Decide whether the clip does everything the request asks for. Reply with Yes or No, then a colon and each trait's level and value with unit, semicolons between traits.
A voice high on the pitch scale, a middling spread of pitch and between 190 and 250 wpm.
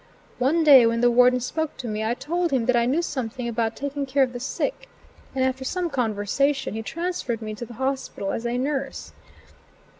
Yes: very high, 255 Hz; average, 3.1 semitones; fast, 205 wpm